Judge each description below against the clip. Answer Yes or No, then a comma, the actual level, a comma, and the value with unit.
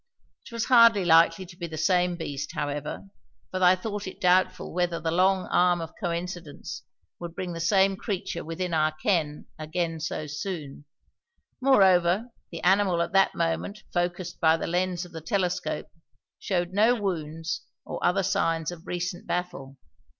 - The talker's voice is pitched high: No, medium, 175 Hz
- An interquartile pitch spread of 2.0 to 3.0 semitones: Yes, narrow, 2.4 semitones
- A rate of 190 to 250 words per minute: No, average, 160 wpm